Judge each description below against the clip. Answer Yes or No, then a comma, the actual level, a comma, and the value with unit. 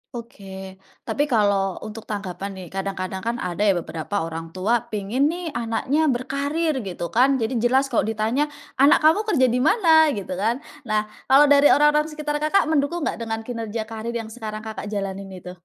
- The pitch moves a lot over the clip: Yes, wide, 6.0 semitones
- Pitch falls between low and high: No, high, 230 Hz